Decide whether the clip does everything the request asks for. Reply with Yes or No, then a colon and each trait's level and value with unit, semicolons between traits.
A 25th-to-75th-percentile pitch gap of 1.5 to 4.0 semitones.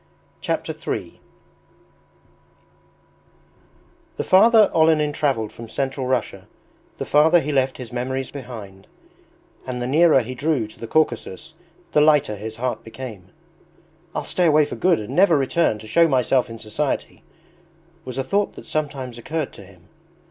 No: average, 5.0 semitones